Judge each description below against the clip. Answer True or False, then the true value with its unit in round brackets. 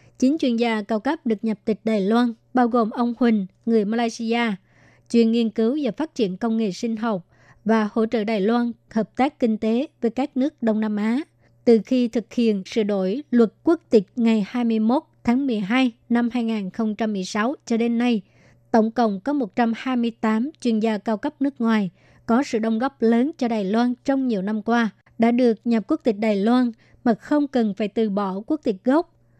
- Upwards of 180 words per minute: True (200 wpm)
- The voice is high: True (230 Hz)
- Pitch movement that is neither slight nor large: False (1.9 semitones)